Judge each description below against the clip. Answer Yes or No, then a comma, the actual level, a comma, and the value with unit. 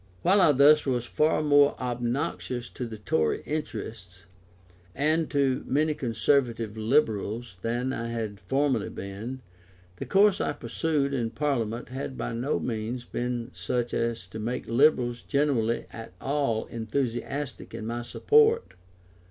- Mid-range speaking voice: No, low, 120 Hz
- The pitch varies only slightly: No, average, 3.8 semitones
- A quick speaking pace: No, slow, 135 wpm